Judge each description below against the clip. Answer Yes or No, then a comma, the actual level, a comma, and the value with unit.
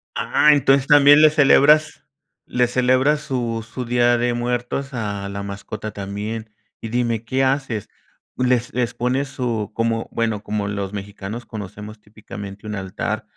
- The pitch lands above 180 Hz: No, low, 115 Hz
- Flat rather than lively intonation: No, average, 3.5 semitones